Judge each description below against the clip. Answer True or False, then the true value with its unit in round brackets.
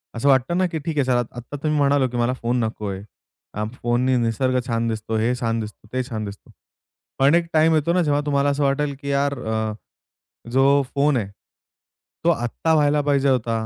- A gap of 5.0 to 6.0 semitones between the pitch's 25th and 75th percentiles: False (3.7 semitones)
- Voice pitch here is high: False (130 Hz)